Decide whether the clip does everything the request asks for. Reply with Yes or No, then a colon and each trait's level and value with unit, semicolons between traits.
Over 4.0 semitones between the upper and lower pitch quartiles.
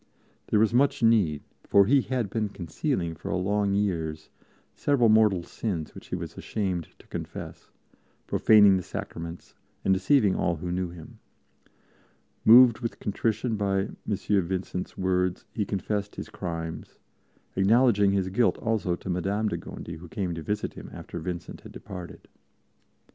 No: average, 3.5 semitones